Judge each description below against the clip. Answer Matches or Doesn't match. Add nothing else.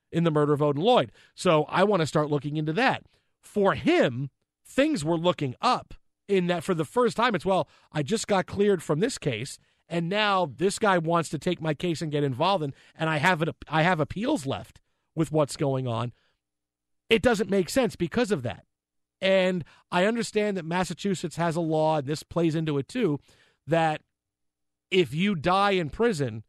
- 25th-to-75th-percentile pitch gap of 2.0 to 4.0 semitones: Doesn't match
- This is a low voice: Doesn't match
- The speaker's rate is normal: Matches